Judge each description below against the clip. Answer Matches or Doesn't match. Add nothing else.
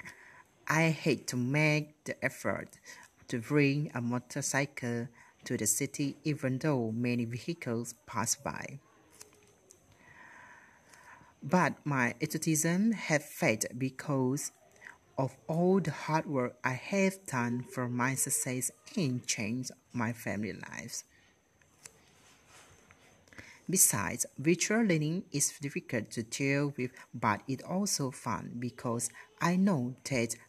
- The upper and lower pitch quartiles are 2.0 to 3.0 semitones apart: Doesn't match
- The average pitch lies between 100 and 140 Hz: Matches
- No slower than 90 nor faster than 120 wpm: Matches